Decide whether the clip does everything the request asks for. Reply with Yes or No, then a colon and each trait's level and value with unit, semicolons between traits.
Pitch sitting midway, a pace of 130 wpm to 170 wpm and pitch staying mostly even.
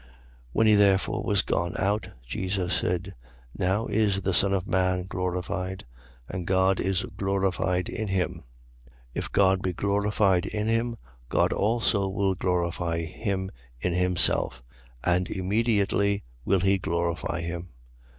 No: very low, 95 Hz; average, 140 wpm; narrow, 1.8 semitones